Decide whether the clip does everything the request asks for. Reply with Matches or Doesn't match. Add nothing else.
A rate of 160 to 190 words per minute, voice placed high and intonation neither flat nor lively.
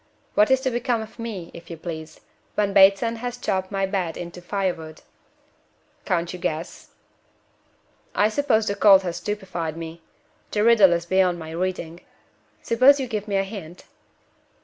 Matches